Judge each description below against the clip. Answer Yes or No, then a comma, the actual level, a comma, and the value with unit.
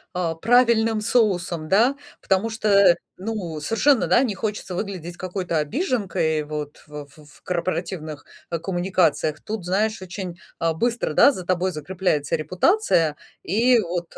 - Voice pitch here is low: No, medium, 185 Hz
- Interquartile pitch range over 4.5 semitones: Yes, average, 5.0 semitones